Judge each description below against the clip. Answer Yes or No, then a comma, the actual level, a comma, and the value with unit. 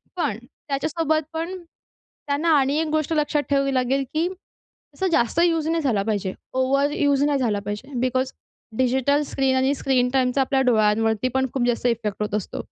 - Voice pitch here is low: No, very high, 265 Hz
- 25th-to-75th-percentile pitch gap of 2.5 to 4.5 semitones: Yes, average, 3.2 semitones